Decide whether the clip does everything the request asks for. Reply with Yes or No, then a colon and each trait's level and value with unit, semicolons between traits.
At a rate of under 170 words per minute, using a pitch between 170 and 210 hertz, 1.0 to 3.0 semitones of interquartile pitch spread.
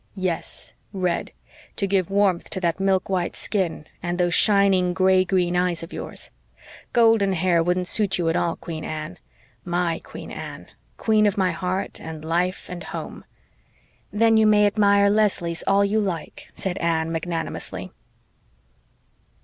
Yes: average, 150 wpm; medium, 185 Hz; narrow, 2.6 semitones